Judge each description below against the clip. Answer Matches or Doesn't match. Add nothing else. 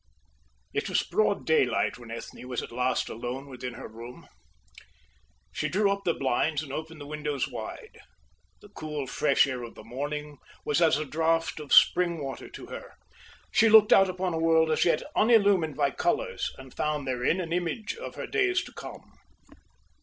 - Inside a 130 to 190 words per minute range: Matches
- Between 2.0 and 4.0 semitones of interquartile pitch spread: Doesn't match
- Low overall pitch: Doesn't match